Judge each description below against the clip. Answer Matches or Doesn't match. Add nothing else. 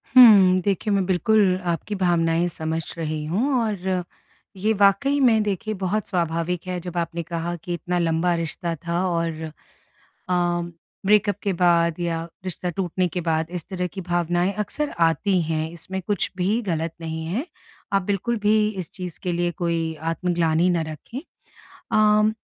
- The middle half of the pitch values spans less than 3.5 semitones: Matches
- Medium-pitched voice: Matches